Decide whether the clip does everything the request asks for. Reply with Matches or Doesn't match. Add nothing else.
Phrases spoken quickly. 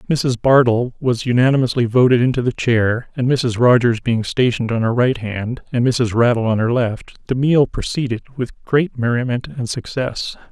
Doesn't match